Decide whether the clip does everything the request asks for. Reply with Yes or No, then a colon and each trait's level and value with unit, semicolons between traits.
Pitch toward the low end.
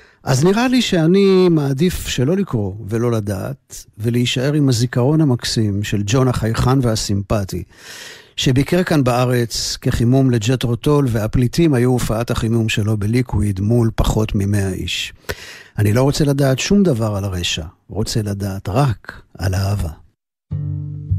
Yes: low, 120 Hz